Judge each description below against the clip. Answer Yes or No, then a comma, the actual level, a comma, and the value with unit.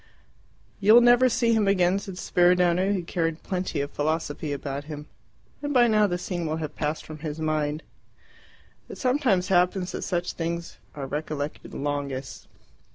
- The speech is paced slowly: No, average, 160 wpm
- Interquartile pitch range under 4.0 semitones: No, average, 4.4 semitones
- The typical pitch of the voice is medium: Yes, medium, 170 Hz